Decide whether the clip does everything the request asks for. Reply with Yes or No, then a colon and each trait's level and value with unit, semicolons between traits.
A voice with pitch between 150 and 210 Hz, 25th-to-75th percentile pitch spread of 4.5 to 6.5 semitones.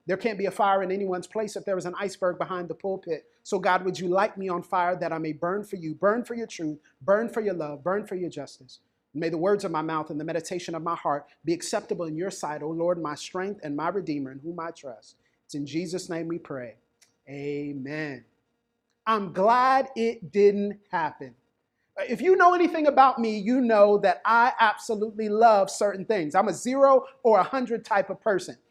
Yes: high, 190 Hz; average, 4.9 semitones